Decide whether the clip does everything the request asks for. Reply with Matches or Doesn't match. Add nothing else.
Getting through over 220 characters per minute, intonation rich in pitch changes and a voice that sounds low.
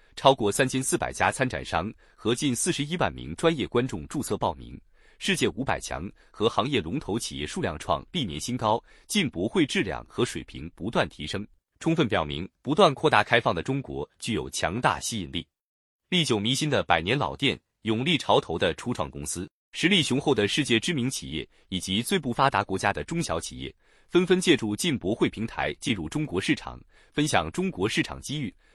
Matches